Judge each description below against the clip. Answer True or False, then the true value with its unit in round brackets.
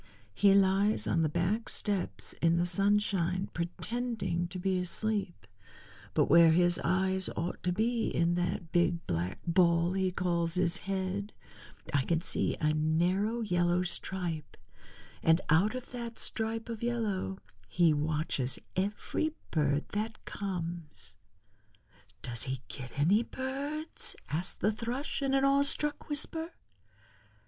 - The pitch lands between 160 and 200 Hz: True (185 Hz)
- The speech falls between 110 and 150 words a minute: True (135 wpm)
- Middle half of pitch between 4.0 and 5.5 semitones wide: True (4.4 semitones)